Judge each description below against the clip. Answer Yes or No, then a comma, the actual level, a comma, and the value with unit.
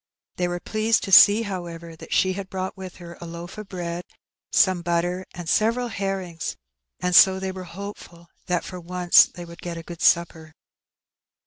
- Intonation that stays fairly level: Yes, narrow, 1.9 semitones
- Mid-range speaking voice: Yes, medium, 180 Hz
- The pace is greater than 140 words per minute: Yes, average, 185 wpm